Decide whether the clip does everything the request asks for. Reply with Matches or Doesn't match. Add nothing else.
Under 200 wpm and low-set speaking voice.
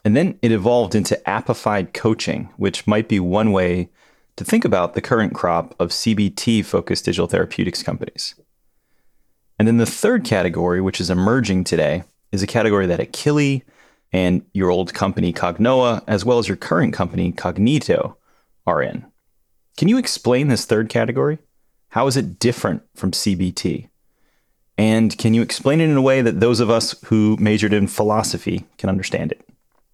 Matches